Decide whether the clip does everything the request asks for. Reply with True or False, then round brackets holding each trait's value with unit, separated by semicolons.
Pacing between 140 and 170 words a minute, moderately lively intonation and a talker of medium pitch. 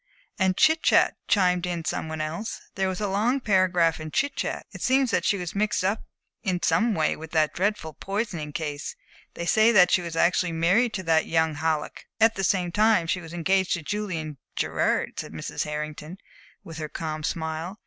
False (200 wpm; 4.2 semitones; 180 Hz)